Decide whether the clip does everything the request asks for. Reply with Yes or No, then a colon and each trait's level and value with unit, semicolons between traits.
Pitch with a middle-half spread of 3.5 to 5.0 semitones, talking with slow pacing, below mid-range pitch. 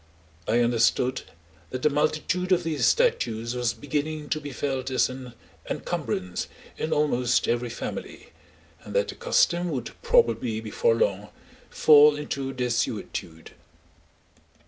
Yes: average, 4.5 semitones; slow, 125 wpm; low, 130 Hz